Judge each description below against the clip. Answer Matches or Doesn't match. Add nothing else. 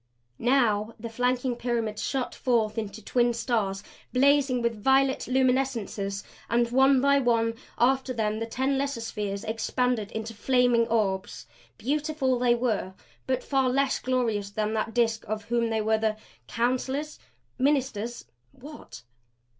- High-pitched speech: Matches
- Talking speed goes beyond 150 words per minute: Doesn't match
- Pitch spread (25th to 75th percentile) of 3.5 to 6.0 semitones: Doesn't match